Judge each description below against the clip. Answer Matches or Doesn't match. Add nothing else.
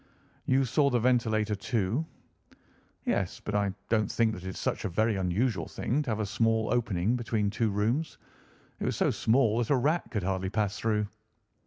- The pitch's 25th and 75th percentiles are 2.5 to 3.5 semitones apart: Matches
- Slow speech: Doesn't match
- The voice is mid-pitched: Doesn't match